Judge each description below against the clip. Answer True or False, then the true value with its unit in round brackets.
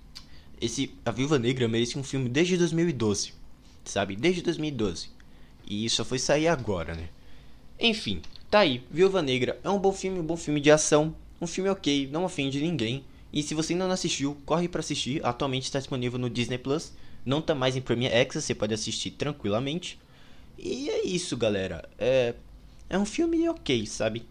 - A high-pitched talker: False (140 Hz)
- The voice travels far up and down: True (6.2 semitones)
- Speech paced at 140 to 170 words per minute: False (185 wpm)